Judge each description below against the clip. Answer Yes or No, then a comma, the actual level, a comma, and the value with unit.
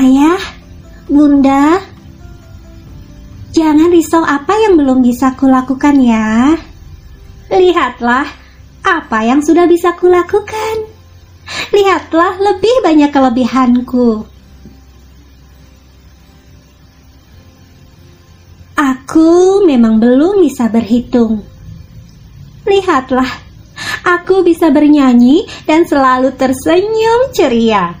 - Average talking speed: No, slow, 70 wpm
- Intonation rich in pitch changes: Yes, wide, 7.4 semitones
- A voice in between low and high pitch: No, very high, 270 Hz